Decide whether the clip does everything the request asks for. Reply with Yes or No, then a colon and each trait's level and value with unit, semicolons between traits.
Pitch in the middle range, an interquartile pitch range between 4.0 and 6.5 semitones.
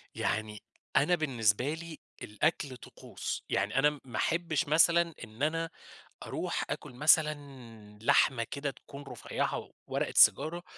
Yes: medium, 145 Hz; average, 4.7 semitones